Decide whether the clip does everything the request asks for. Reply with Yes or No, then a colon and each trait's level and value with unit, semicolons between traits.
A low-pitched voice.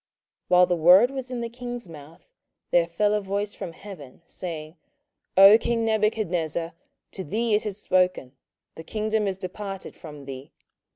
No: high, 195 Hz